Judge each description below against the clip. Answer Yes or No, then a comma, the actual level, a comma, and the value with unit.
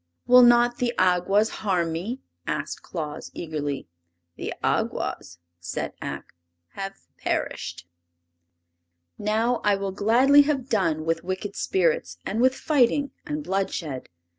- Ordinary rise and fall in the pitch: No, wide, 6.4 semitones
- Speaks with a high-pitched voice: Yes, high, 200 Hz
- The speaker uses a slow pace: Yes, slow, 120 wpm